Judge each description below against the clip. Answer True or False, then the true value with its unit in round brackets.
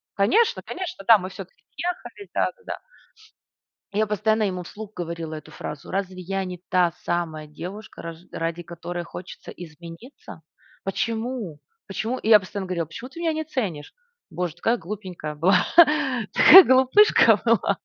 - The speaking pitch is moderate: False (195 Hz)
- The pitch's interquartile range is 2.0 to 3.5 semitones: False (5.3 semitones)